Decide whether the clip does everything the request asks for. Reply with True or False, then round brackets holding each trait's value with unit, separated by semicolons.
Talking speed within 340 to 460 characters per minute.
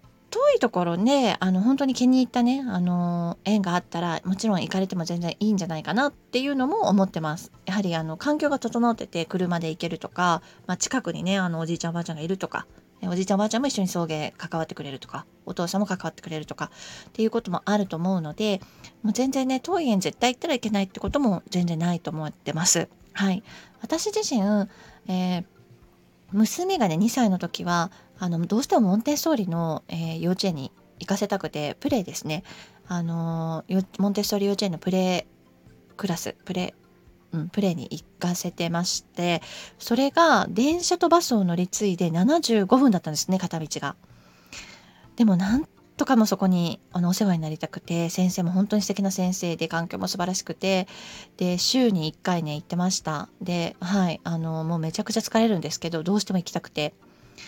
True (380 characters per minute)